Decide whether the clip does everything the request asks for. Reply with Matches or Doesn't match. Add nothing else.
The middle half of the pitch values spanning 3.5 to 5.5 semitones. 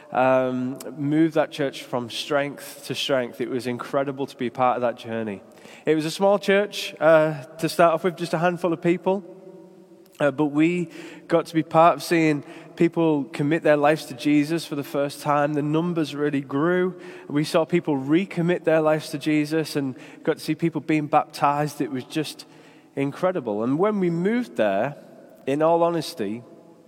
Doesn't match